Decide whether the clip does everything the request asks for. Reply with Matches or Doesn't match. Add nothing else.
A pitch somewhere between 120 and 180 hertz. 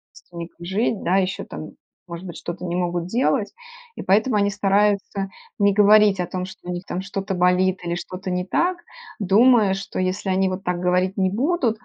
Doesn't match